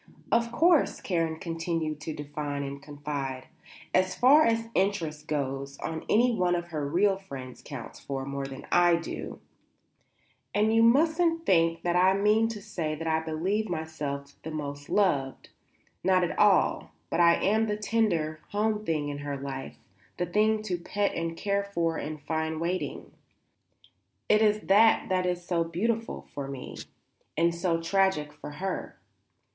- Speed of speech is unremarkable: Yes, average, 160 wpm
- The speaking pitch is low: No, medium, 170 Hz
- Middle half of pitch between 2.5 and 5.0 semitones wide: No, wide, 5.4 semitones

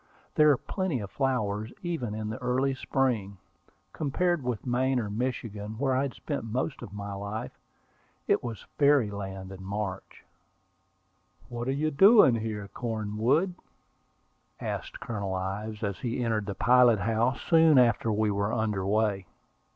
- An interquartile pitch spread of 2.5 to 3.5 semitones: No, average, 4.3 semitones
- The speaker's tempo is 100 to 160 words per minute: Yes, average, 150 wpm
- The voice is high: No, low, 115 Hz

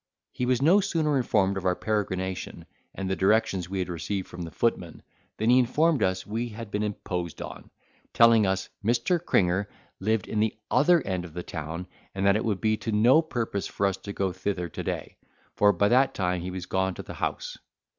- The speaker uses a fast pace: Yes, fast, 210 wpm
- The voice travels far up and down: No, average, 3.9 semitones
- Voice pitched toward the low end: Yes, low, 100 Hz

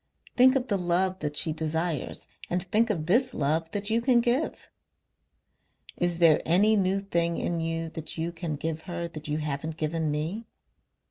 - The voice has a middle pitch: Yes, medium, 170 Hz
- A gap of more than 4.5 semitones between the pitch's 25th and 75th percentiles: No, average, 4.0 semitones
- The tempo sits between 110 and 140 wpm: No, average, 180 wpm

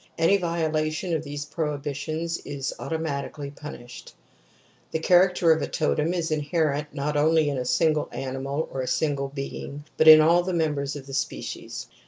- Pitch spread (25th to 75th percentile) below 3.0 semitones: Yes, narrow, 2.4 semitones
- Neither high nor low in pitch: Yes, medium, 150 Hz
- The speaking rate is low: No, average, 165 wpm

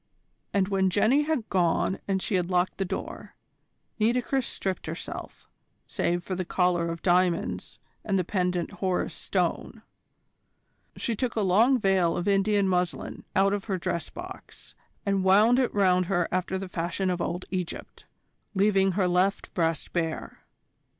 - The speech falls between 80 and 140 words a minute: No, average, 155 wpm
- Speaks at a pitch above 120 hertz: Yes, high, 190 Hz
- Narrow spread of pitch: Yes, narrow, 2.1 semitones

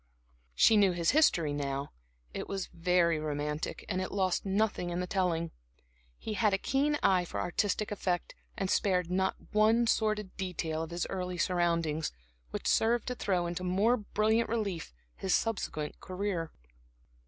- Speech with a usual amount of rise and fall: Yes, average, 3.7 semitones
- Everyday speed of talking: Yes, average, 155 wpm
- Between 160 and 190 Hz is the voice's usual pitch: Yes, medium, 185 Hz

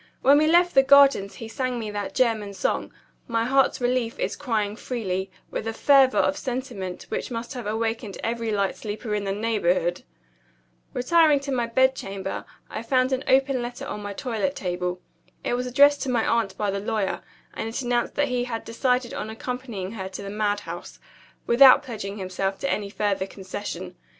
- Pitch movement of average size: Yes, average, 4.1 semitones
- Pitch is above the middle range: Yes, high, 230 Hz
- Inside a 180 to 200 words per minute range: Yes, average, 185 wpm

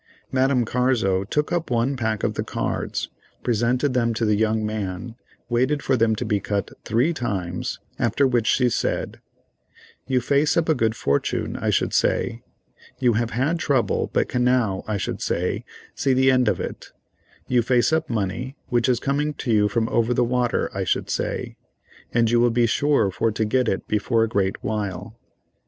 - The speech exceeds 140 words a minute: Yes, average, 185 wpm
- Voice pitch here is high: No, low, 120 Hz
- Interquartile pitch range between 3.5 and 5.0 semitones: No, average, 3.0 semitones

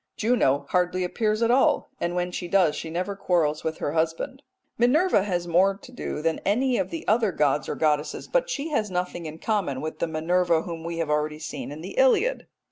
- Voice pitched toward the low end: No, medium, 180 Hz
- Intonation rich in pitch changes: Yes, wide, 5.7 semitones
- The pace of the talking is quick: Yes, fast, 210 wpm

